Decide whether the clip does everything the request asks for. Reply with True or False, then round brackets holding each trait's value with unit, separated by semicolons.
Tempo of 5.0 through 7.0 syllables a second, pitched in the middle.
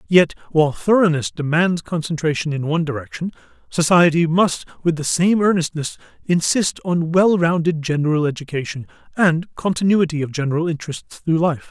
True (5.4 syllables/s; 165 Hz)